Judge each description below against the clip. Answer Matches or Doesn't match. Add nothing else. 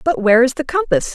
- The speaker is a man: Doesn't match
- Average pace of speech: Doesn't match